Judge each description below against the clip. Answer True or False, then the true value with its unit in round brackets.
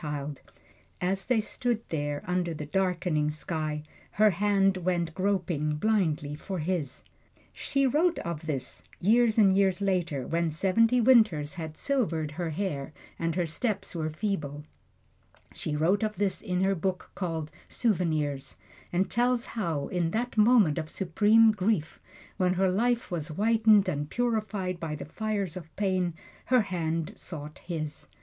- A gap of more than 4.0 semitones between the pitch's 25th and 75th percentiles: True (5.0 semitones)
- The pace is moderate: True (150 wpm)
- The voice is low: False (180 Hz)